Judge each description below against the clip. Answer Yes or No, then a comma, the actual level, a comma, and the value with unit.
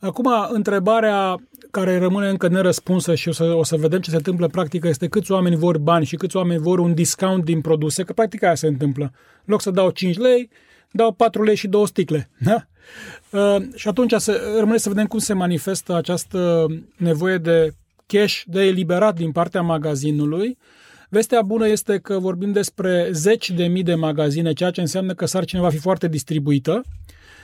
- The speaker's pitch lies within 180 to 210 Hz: Yes, medium, 185 Hz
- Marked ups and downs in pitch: No, average, 3.8 semitones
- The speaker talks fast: Yes, fast, 190 wpm